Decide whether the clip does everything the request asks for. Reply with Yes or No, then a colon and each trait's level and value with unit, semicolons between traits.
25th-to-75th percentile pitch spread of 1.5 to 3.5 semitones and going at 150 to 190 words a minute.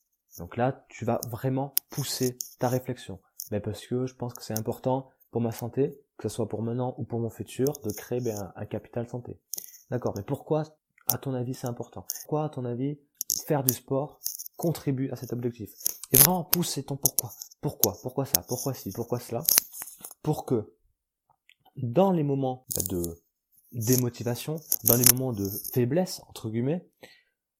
Yes: average, 2.9 semitones; average, 170 wpm